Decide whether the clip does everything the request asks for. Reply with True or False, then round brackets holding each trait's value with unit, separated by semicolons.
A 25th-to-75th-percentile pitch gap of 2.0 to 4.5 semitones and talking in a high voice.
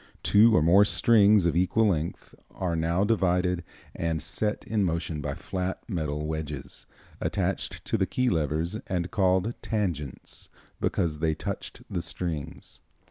False (4.1 semitones; 90 Hz)